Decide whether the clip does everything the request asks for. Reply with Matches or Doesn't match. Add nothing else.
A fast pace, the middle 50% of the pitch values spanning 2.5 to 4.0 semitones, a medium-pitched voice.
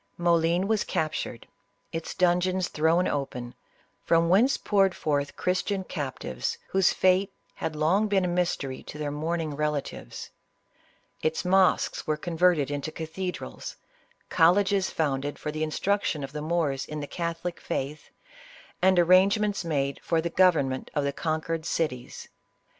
Doesn't match